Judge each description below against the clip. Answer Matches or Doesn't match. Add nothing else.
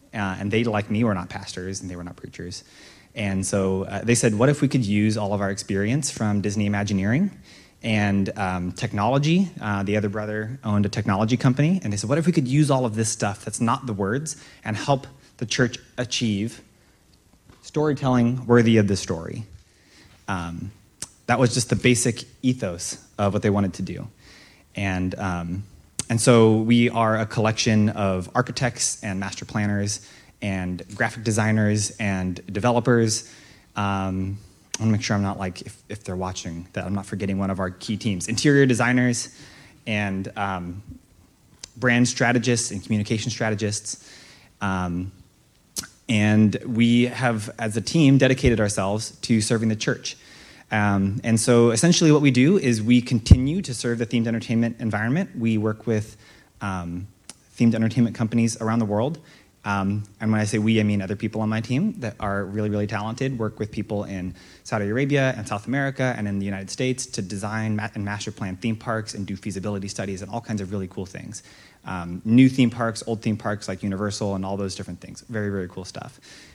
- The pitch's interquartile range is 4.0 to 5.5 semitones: Doesn't match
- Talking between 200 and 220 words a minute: Doesn't match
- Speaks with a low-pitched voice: Matches